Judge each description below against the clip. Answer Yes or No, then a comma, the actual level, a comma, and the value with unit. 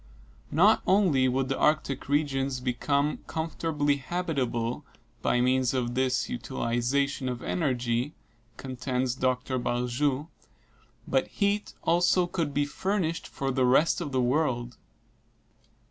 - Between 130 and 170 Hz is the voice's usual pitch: Yes, low, 135 Hz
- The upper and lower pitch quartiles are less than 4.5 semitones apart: Yes, average, 3.4 semitones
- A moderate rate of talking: No, slow, 115 wpm